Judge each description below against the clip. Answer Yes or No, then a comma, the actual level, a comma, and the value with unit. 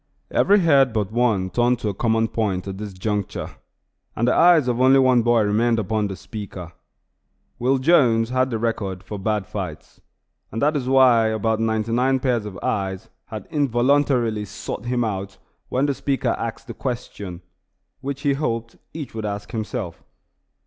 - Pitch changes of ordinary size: Yes, average, 3.6 semitones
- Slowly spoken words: No, average, 170 wpm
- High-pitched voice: No, low, 115 Hz